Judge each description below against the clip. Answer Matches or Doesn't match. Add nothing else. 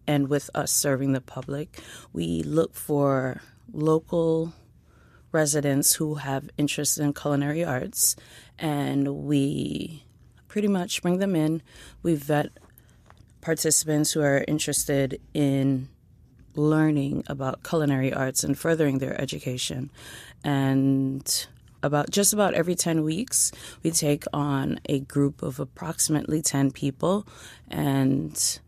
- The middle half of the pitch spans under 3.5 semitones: Matches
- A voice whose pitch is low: Doesn't match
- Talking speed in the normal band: Doesn't match